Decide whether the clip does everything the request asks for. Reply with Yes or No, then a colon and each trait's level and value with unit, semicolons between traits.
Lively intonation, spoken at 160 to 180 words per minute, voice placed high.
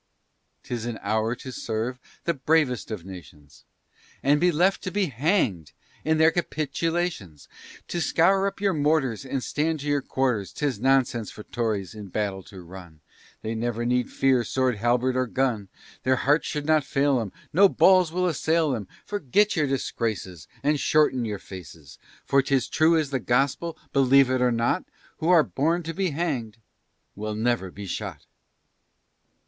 No: wide, 6.1 semitones; average, 165 wpm; low, 130 Hz